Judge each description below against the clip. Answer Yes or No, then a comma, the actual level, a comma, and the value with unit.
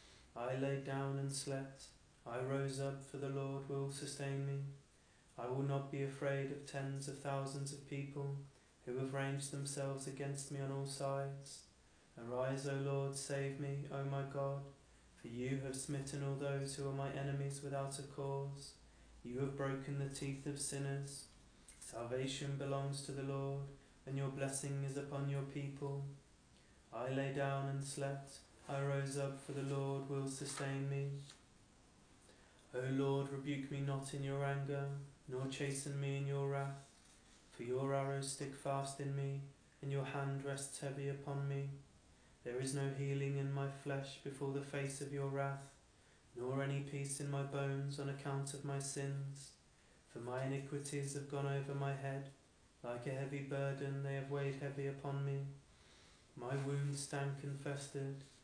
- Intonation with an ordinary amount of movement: No, narrow, 0.3 semitones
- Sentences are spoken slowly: No, average, 165 wpm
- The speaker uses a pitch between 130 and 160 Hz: Yes, medium, 140 Hz